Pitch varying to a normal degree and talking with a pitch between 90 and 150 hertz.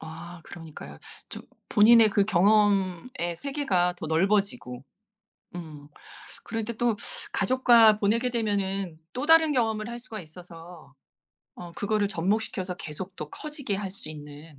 No: average, 4.9 semitones; high, 195 Hz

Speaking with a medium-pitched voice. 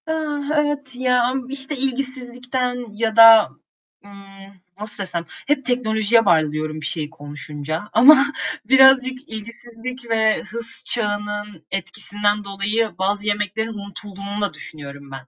No: high, 220 Hz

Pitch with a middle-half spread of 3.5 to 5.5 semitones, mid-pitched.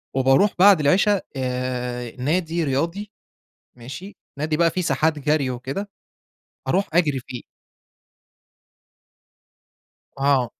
Yes: average, 5.2 semitones; medium, 145 Hz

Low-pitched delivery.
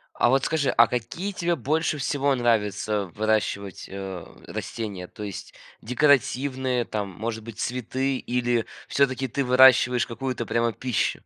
Yes: low, 120 Hz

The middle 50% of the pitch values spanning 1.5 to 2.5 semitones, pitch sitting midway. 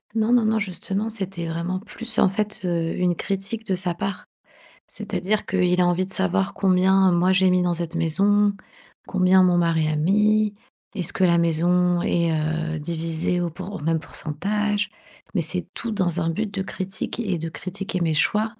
No: average, 2.9 semitones; medium, 180 Hz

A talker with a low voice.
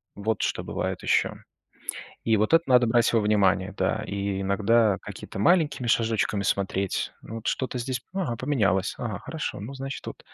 Yes: low, 110 Hz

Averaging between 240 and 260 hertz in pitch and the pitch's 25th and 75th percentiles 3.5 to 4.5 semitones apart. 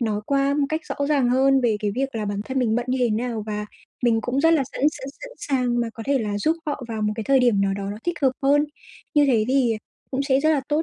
Yes: very high, 255 Hz; average, 3.9 semitones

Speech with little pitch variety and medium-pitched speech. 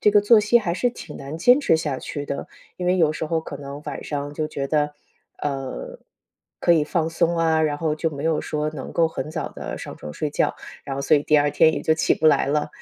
Yes: narrow, 2.3 semitones; medium, 155 Hz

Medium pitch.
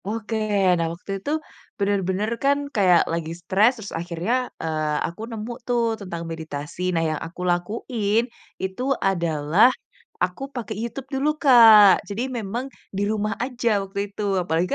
No: high, 200 Hz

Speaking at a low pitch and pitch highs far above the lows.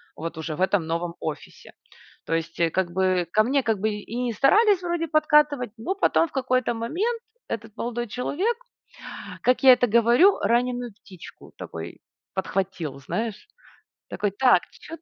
No: high, 235 Hz; wide, 6.4 semitones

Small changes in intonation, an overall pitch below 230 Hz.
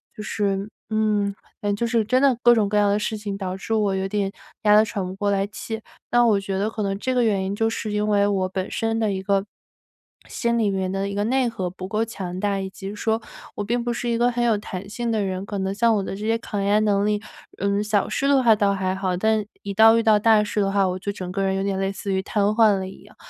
Yes: narrow, 2.2 semitones; high, 205 Hz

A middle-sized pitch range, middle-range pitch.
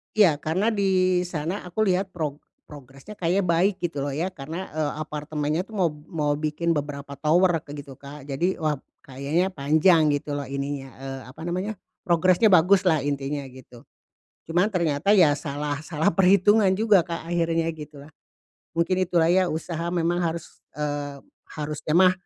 Yes: average, 3.8 semitones; medium, 160 Hz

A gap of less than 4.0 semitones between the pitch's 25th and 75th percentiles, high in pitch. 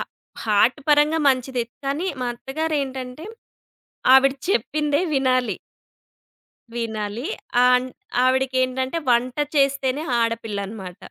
Yes: average, 2.8 semitones; very high, 255 Hz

